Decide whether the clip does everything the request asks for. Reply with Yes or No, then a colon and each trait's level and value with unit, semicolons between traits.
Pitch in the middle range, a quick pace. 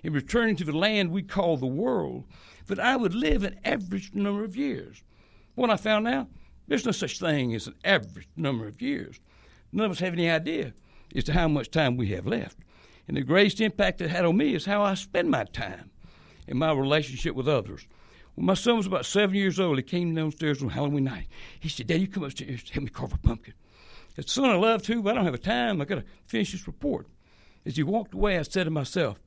Yes: medium, 175 Hz; fast, 240 wpm